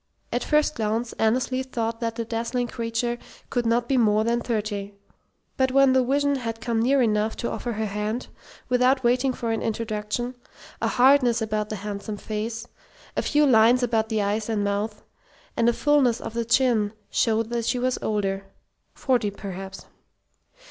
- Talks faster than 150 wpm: Yes, average, 170 wpm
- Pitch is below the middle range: No, high, 230 Hz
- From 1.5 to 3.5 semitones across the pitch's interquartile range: Yes, narrow, 2.6 semitones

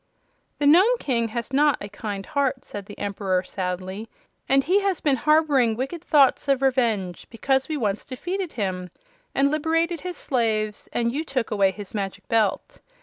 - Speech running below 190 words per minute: Yes, average, 170 wpm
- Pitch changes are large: Yes, wide, 6.4 semitones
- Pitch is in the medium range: No, very high, 255 Hz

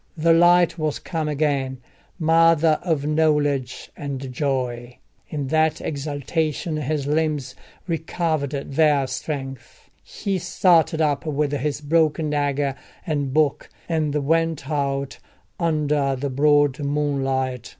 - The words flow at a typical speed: No, slow, 115 wpm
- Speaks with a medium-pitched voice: Yes, medium, 150 Hz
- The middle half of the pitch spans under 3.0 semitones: Yes, narrow, 2.5 semitones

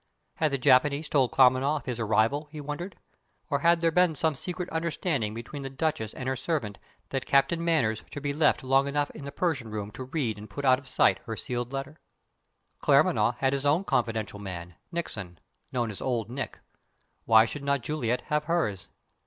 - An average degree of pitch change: Yes, average, 4.7 semitones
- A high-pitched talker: No, low, 135 Hz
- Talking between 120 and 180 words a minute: No, average, 195 wpm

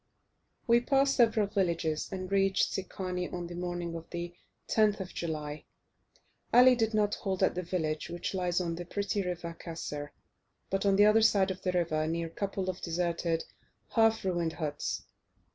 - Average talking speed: Yes, average, 175 wpm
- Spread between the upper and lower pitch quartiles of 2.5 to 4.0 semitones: Yes, average, 3.1 semitones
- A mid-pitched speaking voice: Yes, medium, 180 Hz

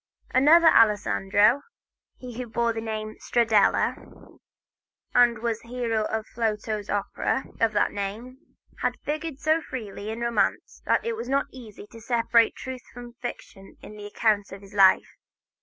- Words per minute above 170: No, average, 150 wpm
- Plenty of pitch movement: No, average, 2.8 semitones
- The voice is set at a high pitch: Yes, high, 230 Hz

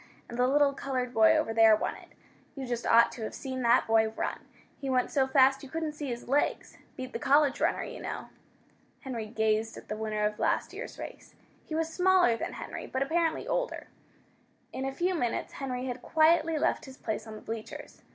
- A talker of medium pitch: No, very high, 260 Hz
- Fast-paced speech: Yes, fast, 210 wpm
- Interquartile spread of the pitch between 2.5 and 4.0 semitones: No, average, 4.4 semitones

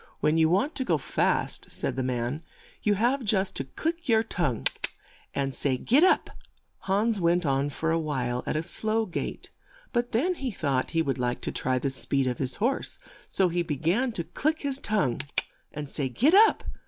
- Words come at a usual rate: No, fast, 215 wpm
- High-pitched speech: No, medium, 170 Hz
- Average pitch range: No, wide, 8.9 semitones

